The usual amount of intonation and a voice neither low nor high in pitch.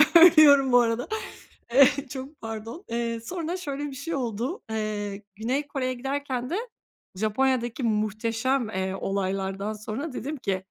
No: average, 4.5 semitones; high, 245 Hz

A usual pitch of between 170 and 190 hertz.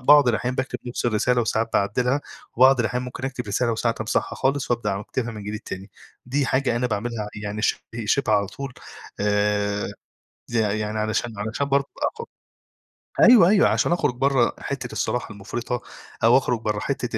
No: low, 120 Hz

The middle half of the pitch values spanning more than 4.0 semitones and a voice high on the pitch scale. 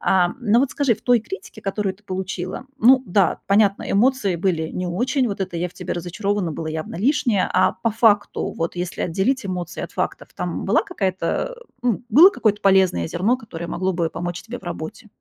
Yes: average, 4.7 semitones; high, 195 Hz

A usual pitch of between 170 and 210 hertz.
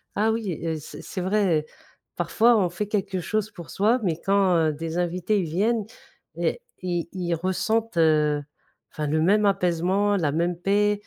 Yes: medium, 185 Hz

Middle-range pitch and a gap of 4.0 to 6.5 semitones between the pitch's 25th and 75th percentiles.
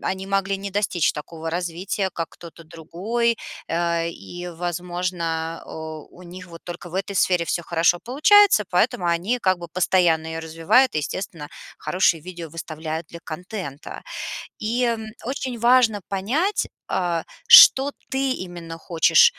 No: medium, 175 Hz; average, 3.6 semitones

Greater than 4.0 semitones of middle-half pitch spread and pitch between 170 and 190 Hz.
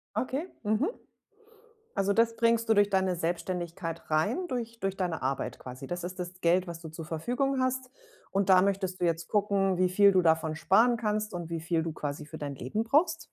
Yes: average, 5.1 semitones; medium, 185 Hz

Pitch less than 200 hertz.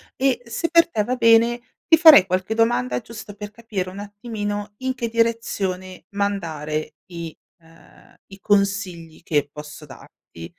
No: high, 205 Hz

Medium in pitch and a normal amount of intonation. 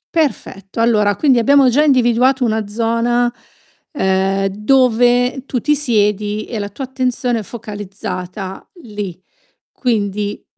No: high, 230 Hz; average, 3.6 semitones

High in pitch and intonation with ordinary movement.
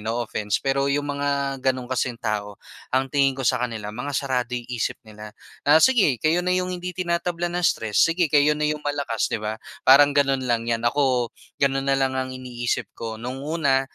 No: low, 135 Hz; average, 3.4 semitones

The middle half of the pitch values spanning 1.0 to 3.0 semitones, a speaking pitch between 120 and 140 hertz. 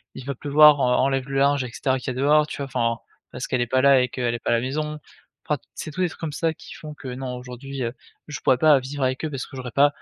Yes: narrow, 2.4 semitones; low, 135 Hz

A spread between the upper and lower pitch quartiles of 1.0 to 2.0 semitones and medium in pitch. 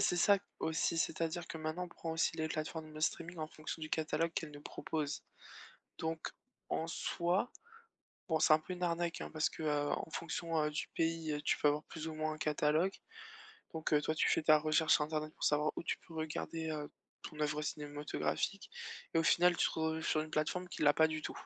Yes: narrow, 1.3 semitones; medium, 160 Hz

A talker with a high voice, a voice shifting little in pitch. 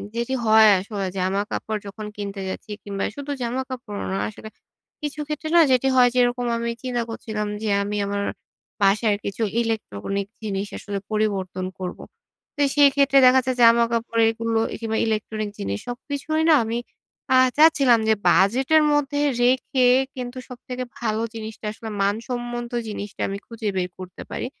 No: high, 225 Hz; average, 3.6 semitones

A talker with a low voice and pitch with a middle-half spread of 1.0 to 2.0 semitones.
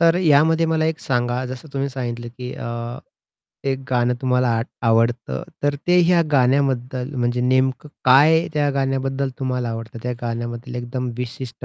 No: low, 130 Hz; narrow, 2.5 semitones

